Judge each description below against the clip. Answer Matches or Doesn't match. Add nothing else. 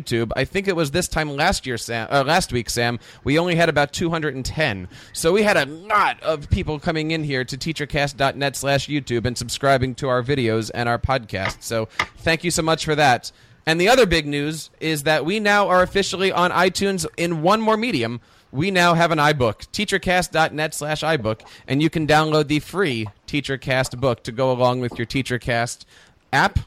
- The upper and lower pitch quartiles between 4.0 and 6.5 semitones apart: Matches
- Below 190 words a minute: Doesn't match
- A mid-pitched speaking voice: Matches